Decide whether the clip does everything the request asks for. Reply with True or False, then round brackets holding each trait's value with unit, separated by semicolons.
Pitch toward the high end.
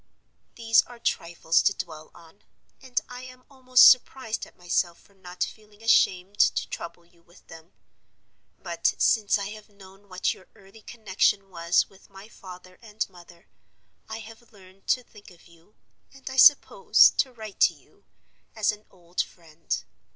True (195 Hz)